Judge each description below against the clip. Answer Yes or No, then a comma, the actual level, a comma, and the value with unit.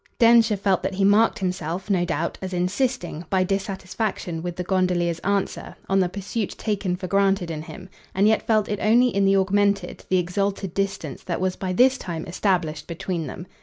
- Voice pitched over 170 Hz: Yes, high, 190 Hz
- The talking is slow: No, average, 190 wpm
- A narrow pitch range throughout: Yes, narrow, 2.2 semitones